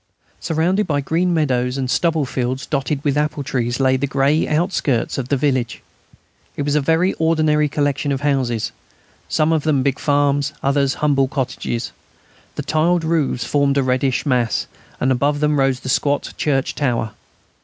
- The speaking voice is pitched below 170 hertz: Yes, medium, 140 Hz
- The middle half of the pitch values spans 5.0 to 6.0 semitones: No, narrow, 2.5 semitones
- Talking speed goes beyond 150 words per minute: Yes, average, 165 wpm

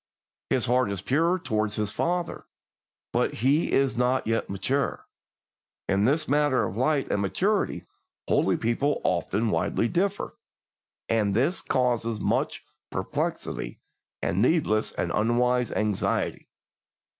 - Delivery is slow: Yes, slow, 120 wpm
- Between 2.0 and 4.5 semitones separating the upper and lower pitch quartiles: No, average, 5.1 semitones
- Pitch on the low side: Yes, low, 125 Hz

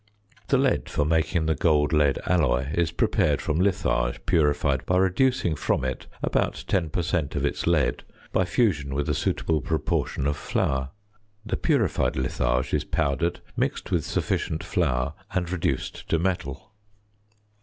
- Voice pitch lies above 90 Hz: No, very low, 80 Hz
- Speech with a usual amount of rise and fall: Yes, average, 4.0 semitones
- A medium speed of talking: Yes, average, 155 wpm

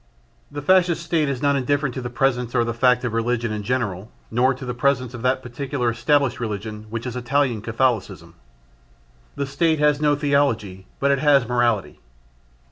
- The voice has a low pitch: Yes, low, 125 Hz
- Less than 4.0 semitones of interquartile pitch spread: Yes, average, 3.3 semitones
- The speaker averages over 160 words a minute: Yes, average, 180 wpm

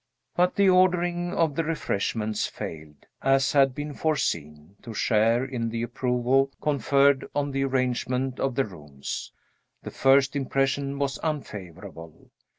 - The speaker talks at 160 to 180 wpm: No, slow, 135 wpm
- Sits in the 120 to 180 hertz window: Yes, low, 135 Hz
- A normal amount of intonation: Yes, average, 4.2 semitones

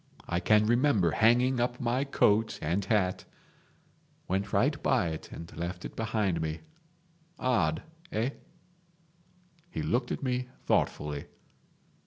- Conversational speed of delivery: No, slow, 125 wpm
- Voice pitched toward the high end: No, low, 110 Hz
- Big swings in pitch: Yes, wide, 6.2 semitones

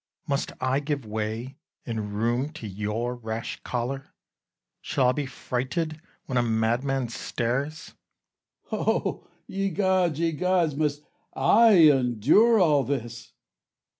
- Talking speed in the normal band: No, slow, 125 wpm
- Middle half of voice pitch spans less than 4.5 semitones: No, average, 4.8 semitones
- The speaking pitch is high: No, low, 135 Hz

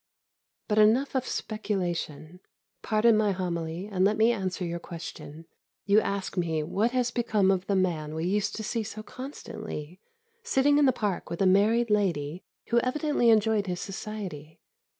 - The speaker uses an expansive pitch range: No, average, 4.1 semitones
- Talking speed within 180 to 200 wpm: No, average, 165 wpm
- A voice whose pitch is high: Yes, high, 205 Hz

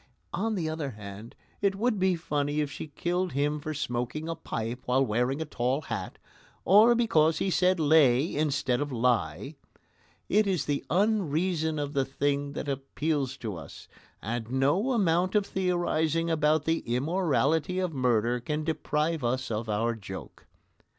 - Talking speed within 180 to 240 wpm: No, average, 160 wpm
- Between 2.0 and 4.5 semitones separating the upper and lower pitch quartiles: No, average, 4.9 semitones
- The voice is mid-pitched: Yes, medium, 150 Hz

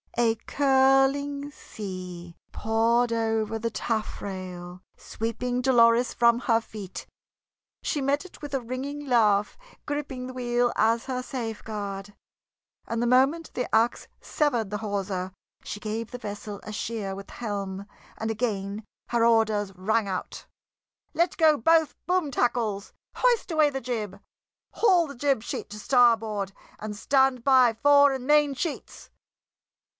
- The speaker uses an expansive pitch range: No, average, 4.3 semitones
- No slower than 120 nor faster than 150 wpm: Yes, average, 140 wpm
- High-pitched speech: Yes, high, 230 Hz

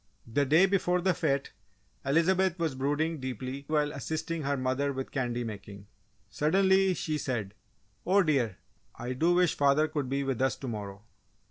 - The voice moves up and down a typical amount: Yes, average, 4.4 semitones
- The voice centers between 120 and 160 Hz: Yes, medium, 140 Hz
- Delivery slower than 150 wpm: No, average, 160 wpm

